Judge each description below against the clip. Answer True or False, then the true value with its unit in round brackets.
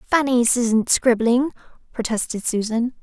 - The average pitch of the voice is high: True (240 Hz)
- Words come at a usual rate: False (100 wpm)